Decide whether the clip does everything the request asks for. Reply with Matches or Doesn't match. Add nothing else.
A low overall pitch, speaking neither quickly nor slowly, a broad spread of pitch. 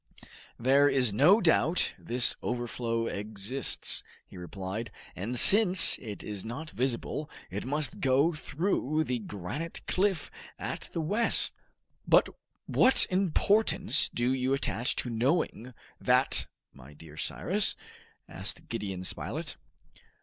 Doesn't match